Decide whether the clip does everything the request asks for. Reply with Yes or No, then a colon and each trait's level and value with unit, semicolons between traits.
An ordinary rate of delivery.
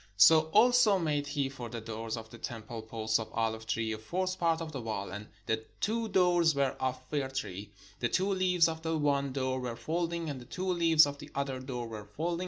No: fast, 225 wpm